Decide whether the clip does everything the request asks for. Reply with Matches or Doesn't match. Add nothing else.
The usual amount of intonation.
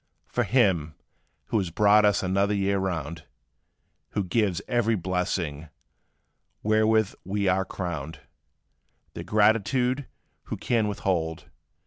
Matches